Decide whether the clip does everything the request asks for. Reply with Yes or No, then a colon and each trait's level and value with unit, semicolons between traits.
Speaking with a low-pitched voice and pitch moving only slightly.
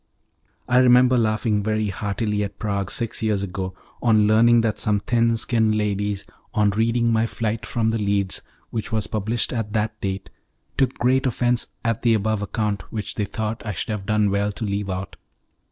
Yes: low, 110 Hz; narrow, 2.0 semitones